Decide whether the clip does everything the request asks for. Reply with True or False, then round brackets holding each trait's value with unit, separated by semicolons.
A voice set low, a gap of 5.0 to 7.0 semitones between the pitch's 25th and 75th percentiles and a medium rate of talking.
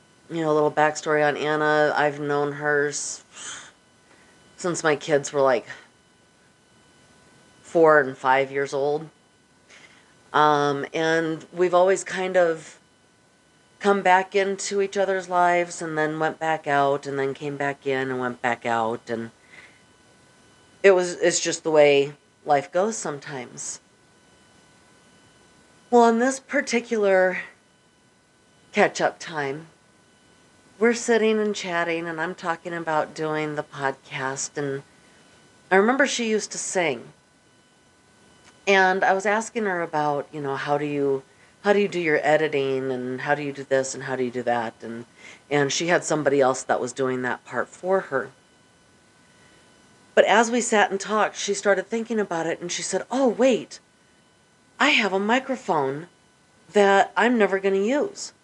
False (160 Hz; 5.4 semitones; 150 wpm)